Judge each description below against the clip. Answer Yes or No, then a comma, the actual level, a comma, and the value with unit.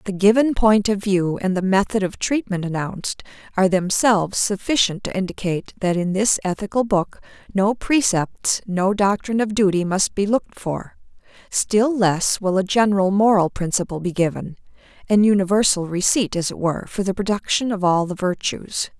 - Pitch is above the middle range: Yes, high, 195 Hz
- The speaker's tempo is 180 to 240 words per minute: No, average, 165 wpm